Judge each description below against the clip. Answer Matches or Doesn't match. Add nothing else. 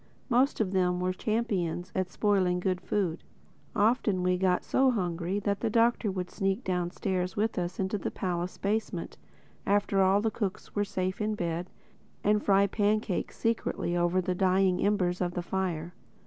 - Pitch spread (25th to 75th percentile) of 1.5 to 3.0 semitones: Matches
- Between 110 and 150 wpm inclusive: Doesn't match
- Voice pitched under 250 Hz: Matches